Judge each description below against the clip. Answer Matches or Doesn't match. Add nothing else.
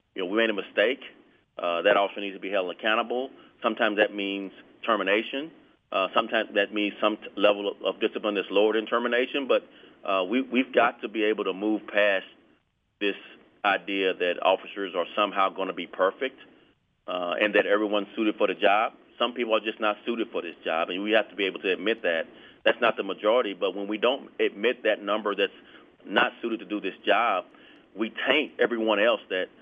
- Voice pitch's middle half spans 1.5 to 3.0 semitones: Matches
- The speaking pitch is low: Matches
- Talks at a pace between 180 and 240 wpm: Matches